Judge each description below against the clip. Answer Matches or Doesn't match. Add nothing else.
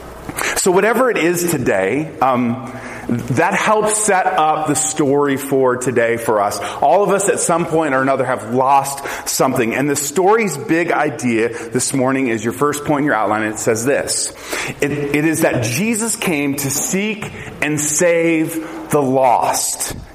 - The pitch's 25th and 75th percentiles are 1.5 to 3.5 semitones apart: Doesn't match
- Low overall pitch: Doesn't match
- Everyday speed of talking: Matches